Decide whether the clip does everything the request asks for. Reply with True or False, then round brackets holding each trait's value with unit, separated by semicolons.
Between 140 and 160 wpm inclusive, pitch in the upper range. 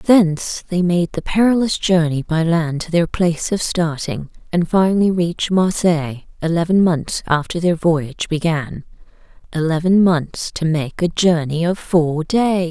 False (150 wpm; 170 Hz)